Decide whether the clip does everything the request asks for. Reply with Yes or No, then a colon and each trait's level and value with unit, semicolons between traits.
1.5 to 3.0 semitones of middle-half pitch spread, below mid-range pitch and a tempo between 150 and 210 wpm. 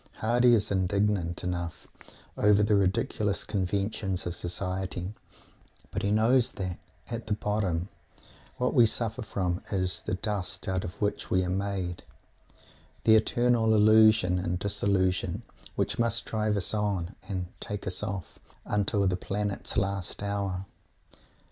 No: narrow, 2.6 semitones; low, 100 Hz; average, 140 wpm